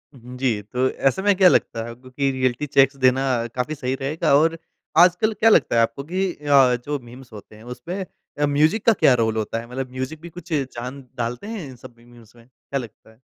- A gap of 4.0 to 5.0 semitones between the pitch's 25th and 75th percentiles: Yes, average, 4.3 semitones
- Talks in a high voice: No, low, 130 Hz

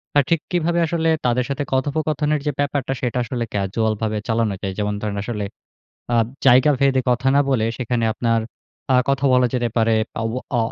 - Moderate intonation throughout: Yes, average, 3.9 semitones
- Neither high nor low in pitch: No, low, 125 Hz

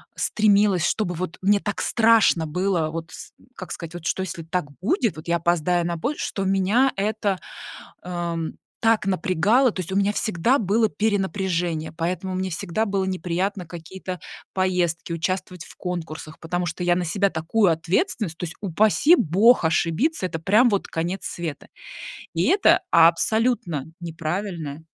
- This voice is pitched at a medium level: Yes, medium, 180 Hz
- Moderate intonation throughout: Yes, average, 3.4 semitones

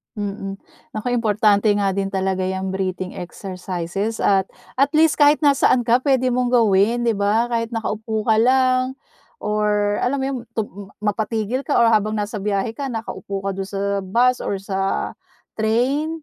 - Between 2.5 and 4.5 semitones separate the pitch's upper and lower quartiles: Yes, average, 3.7 semitones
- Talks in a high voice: Yes, high, 215 Hz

